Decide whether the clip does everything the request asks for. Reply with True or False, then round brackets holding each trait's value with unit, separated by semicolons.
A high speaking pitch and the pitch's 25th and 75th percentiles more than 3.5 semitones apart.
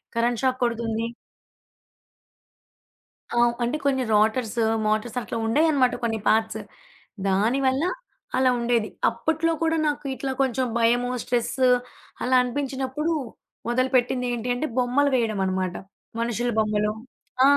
False (245 Hz; 2.8 semitones)